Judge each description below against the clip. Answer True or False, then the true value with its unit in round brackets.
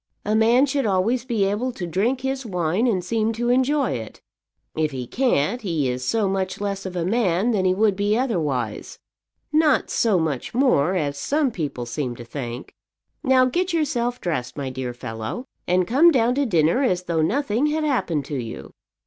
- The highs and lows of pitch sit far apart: True (8.2 semitones)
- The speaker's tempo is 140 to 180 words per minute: False (190 wpm)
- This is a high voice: True (200 Hz)